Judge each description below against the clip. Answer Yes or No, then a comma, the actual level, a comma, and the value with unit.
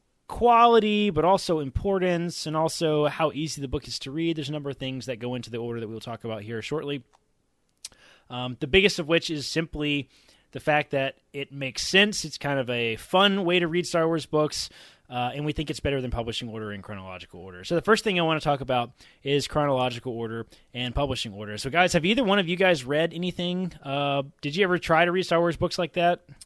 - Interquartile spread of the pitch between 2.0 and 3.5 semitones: No, wide, 5.5 semitones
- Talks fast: Yes, fast, 230 wpm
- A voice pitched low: No, medium, 150 Hz